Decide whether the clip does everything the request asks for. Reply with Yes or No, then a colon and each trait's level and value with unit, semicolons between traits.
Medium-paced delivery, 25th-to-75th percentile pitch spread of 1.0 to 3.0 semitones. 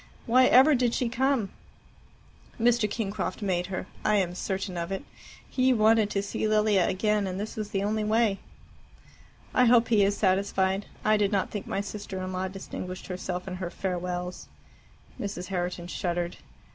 Yes: average, 170 wpm; average, 2.7 semitones